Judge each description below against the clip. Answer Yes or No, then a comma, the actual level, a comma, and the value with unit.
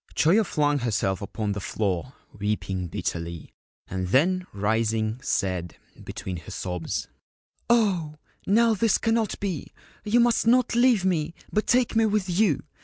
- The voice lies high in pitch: No, medium, 150 Hz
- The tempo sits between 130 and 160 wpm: Yes, average, 145 wpm